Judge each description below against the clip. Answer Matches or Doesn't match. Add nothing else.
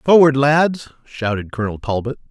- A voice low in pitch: Matches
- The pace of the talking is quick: Doesn't match